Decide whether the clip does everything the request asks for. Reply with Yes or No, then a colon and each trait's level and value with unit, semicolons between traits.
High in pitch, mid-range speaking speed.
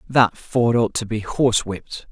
No: low, 115 Hz; average, 170 wpm